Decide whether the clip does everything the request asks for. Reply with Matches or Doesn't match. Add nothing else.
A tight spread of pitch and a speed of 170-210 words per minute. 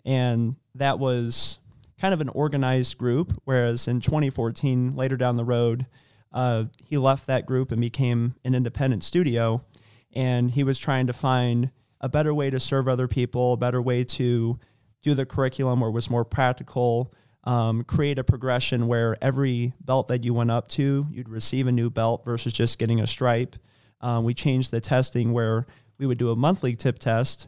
Matches